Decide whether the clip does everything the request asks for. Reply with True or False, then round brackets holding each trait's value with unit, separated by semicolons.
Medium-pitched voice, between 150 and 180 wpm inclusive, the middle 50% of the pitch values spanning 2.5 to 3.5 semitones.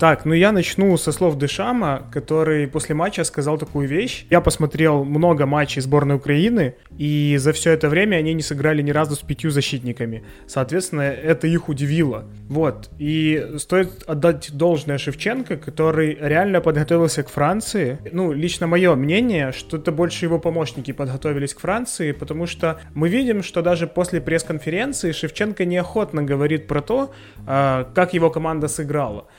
True (155 Hz; 155 wpm; 2.9 semitones)